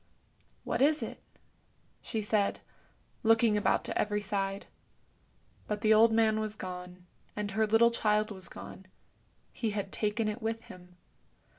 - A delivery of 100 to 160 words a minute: Yes, average, 155 wpm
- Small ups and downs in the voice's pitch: Yes, narrow, 1.9 semitones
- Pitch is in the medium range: No, high, 210 Hz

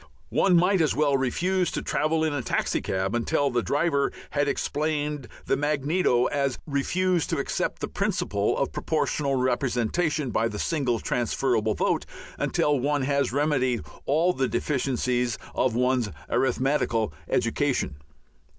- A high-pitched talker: No, medium, 140 Hz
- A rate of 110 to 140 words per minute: Yes, slow, 135 wpm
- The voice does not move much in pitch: No, average, 3.5 semitones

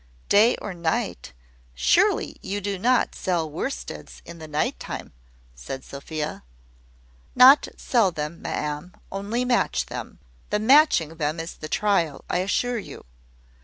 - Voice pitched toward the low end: No, medium, 180 Hz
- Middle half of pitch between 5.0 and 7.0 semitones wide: Yes, wide, 5.6 semitones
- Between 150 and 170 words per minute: No, slow, 135 wpm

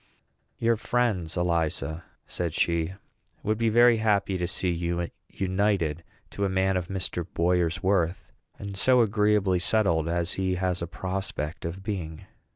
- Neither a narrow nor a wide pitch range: Yes, average, 3.0 semitones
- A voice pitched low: Yes, very low, 95 Hz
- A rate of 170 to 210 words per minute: No, average, 150 wpm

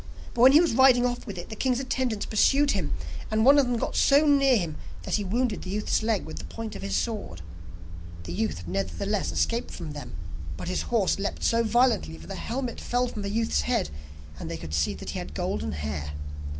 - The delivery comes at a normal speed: No, fast, 225 wpm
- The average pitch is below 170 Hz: No, high, 215 Hz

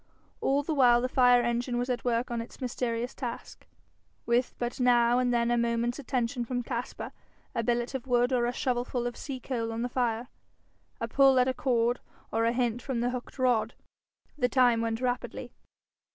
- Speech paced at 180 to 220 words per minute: Yes, average, 195 wpm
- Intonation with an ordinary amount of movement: No, narrow, 1.2 semitones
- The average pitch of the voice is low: No, high, 245 Hz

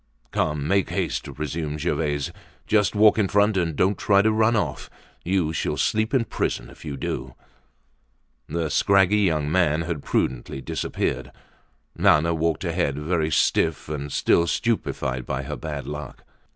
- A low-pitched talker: Yes, very low, 80 Hz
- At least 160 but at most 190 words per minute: No, average, 150 wpm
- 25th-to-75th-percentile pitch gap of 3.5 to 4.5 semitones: No, average, 5.0 semitones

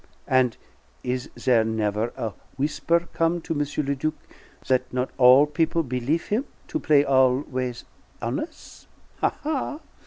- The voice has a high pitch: No, low, 135 Hz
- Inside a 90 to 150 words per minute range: Yes, slow, 135 wpm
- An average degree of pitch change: Yes, average, 4.2 semitones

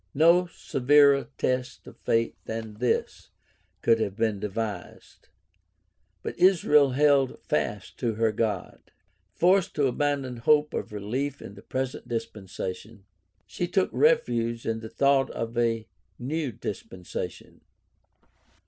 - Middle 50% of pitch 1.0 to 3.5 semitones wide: No, average, 4.3 semitones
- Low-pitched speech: Yes, low, 120 Hz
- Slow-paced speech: Yes, slow, 120 wpm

